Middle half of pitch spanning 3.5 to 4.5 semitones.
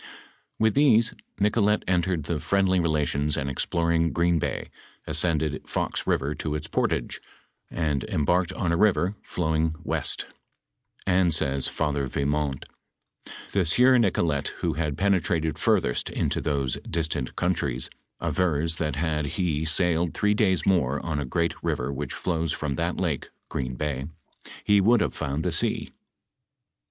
Yes: average, 3.8 semitones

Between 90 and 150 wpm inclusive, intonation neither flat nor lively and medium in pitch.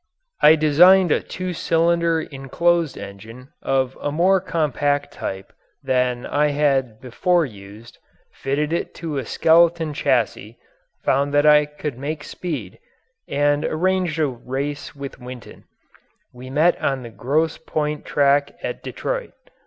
Yes: slow, 135 wpm; average, 3.9 semitones; medium, 145 Hz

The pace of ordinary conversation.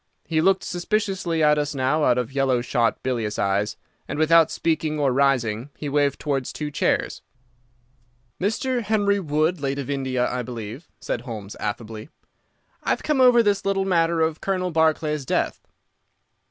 Yes: average, 155 wpm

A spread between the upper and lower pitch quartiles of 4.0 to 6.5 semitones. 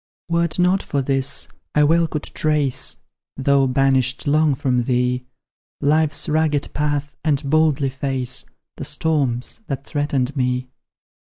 No: average, 2.7 semitones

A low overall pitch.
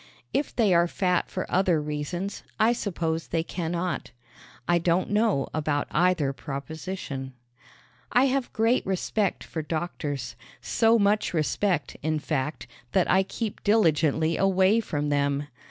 No: medium, 175 Hz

